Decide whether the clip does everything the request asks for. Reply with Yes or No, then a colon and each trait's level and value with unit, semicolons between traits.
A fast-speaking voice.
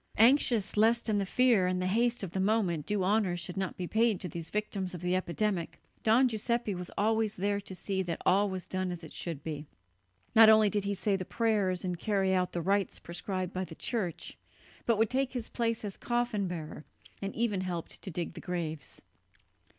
Yes: fast, 210 wpm